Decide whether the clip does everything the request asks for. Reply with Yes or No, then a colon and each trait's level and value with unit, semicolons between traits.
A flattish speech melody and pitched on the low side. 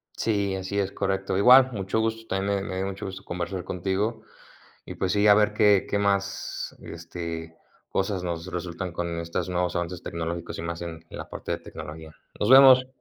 No: average, 3.0 semitones; very low, 95 Hz